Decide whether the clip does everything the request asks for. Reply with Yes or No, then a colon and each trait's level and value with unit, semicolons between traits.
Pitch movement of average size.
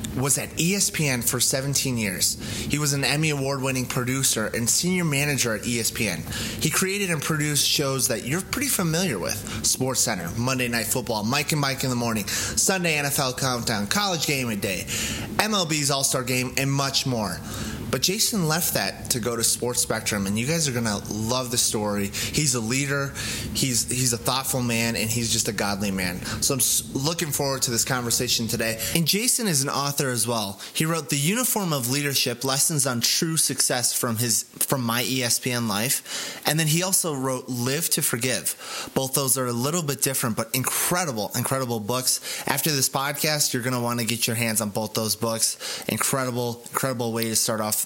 Yes: average, 3.9 semitones